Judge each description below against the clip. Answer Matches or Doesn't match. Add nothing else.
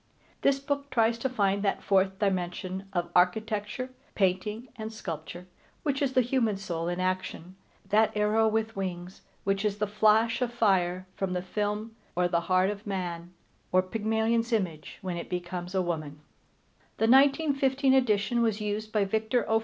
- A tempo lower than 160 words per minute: Doesn't match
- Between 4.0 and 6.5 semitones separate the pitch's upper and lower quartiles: Doesn't match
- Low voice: Doesn't match